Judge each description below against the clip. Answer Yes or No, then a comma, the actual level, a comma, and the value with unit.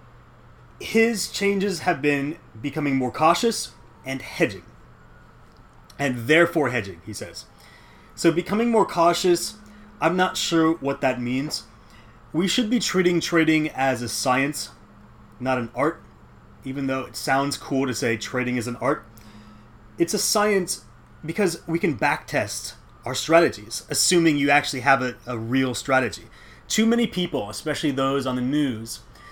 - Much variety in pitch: Yes, wide, 5.7 semitones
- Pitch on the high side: No, medium, 140 Hz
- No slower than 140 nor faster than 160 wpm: Yes, average, 145 wpm